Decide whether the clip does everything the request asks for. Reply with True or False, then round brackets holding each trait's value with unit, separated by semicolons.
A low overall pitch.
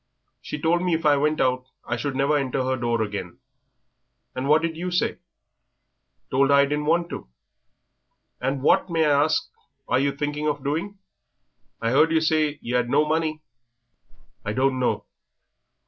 False (145 Hz)